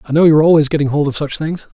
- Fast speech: Yes, fast, 300 wpm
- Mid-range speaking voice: Yes, medium, 150 Hz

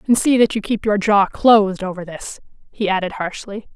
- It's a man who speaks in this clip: No, female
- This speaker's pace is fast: Yes, fast, 210 wpm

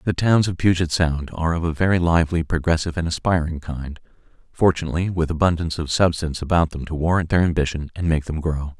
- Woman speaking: No, male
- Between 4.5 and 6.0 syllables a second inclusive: No, 6.4 syllables/s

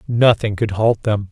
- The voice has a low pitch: Yes, low, 105 Hz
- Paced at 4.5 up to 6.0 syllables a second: No, 4.3 syllables/s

